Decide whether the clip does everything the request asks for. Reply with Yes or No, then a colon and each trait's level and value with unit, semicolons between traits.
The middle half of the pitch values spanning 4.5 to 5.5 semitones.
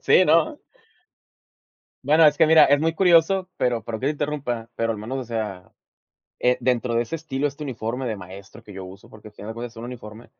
Yes: average, 5.1 semitones